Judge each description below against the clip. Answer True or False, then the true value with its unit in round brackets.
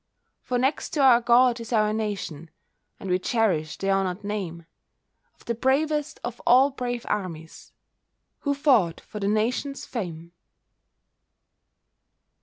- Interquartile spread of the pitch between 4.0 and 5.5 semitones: True (5.2 semitones)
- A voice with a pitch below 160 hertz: False (220 Hz)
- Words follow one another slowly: True (130 wpm)